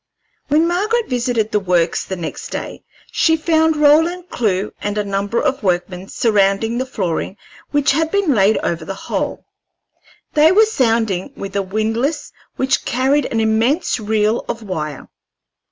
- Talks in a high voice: Yes, high, 225 Hz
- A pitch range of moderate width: No, wide, 7.1 semitones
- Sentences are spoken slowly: No, average, 155 wpm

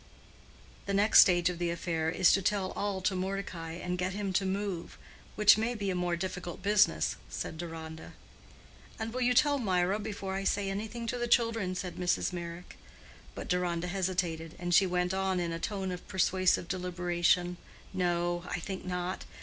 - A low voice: No, medium, 185 Hz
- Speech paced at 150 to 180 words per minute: Yes, average, 175 wpm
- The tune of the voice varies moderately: No, narrow, 2.2 semitones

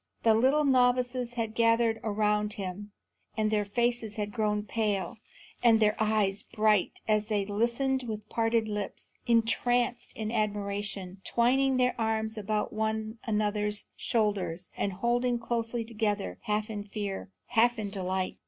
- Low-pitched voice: No, high, 220 Hz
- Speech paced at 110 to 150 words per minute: Yes, average, 140 wpm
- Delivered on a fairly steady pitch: Yes, narrow, 2.1 semitones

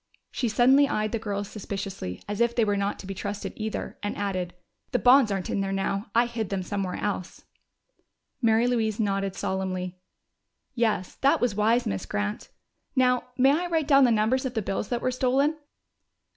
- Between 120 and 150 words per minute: No, average, 185 wpm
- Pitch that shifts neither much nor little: Yes, average, 3.9 semitones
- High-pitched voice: Yes, high, 215 Hz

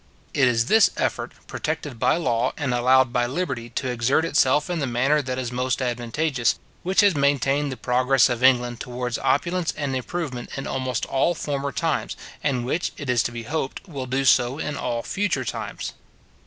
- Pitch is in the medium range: No, low, 130 Hz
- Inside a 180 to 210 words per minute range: Yes, average, 185 wpm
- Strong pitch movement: No, average, 3.1 semitones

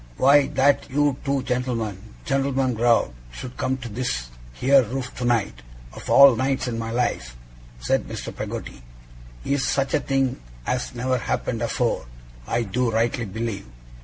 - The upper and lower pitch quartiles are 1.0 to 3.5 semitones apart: Yes, average, 2.9 semitones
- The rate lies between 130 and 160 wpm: Yes, average, 150 wpm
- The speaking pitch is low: Yes, low, 125 Hz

